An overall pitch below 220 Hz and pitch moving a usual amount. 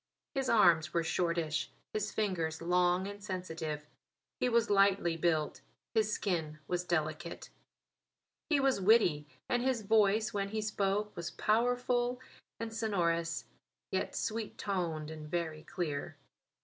Yes: medium, 185 Hz; average, 4.7 semitones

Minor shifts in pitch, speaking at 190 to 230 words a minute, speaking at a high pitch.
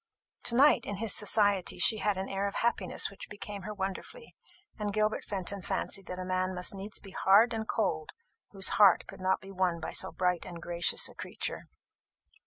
Yes: narrow, 2.3 semitones; average, 195 wpm; high, 195 Hz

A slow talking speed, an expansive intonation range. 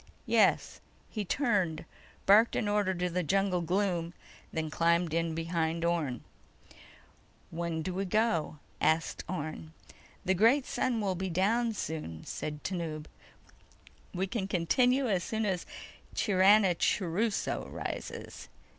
No: slow, 120 wpm; average, 3.8 semitones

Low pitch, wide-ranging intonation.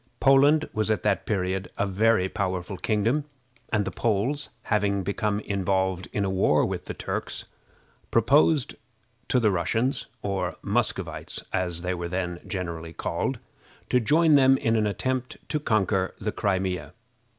No: low, 100 Hz; average, 4.0 semitones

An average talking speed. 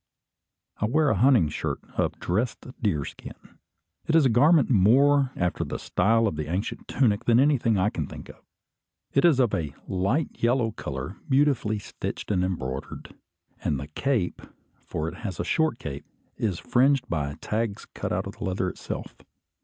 Yes: average, 170 wpm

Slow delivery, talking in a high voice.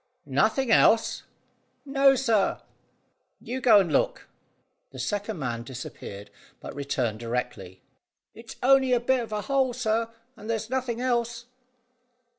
Yes: slow, 130 wpm; high, 225 Hz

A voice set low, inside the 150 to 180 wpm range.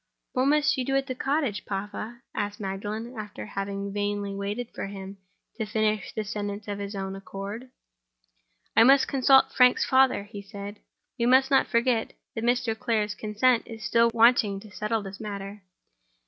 No: high, 215 Hz; average, 170 wpm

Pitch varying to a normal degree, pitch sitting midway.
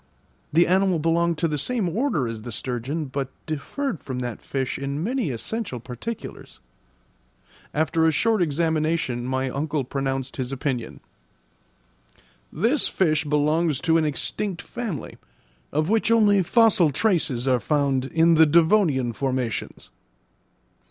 Yes: average, 4.9 semitones; medium, 155 Hz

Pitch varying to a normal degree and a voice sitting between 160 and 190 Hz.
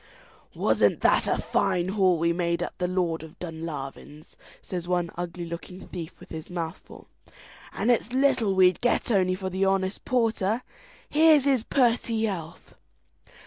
Yes: average, 4.5 semitones; medium, 185 Hz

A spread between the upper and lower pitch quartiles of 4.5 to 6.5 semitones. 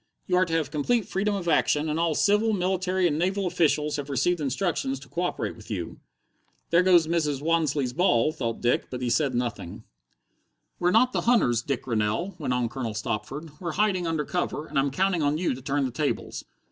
Yes: average, 5.3 semitones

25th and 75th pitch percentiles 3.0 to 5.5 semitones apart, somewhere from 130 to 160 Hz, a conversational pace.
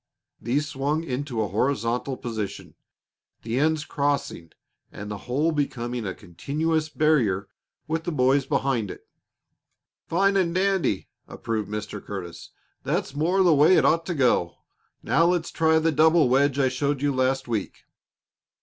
Yes: average, 5.2 semitones; medium, 140 Hz; average, 150 wpm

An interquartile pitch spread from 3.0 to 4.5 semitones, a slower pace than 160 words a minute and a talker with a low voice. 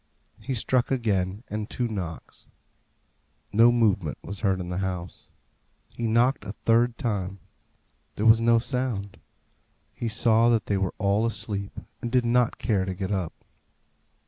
Yes: average, 3.4 semitones; average, 150 wpm; low, 110 Hz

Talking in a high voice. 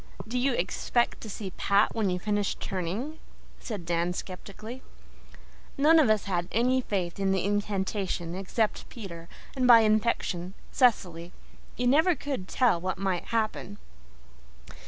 Yes: high, 205 Hz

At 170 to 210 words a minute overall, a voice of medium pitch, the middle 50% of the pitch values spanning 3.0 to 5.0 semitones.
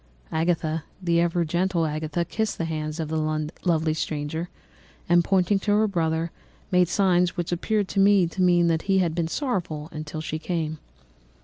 No: average, 175 wpm; medium, 170 Hz; narrow, 2.4 semitones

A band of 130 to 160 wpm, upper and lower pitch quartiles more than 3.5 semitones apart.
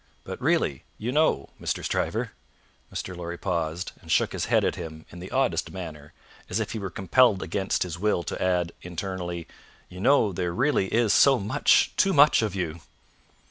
No: average, 185 wpm; average, 4.5 semitones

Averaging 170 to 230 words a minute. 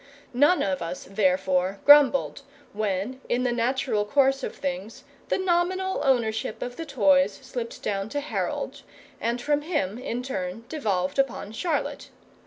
No: average, 145 wpm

